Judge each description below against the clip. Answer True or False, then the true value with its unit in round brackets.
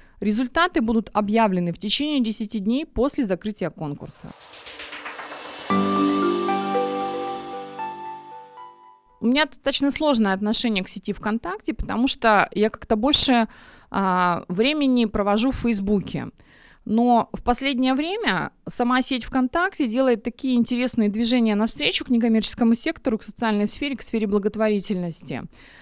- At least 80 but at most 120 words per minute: True (115 wpm)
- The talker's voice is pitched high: True (225 Hz)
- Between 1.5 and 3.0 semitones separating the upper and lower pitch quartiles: False (4.4 semitones)